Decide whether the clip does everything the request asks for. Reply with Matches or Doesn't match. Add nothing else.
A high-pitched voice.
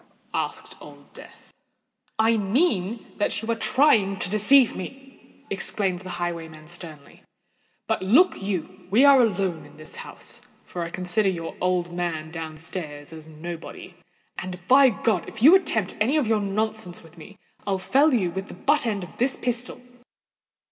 Matches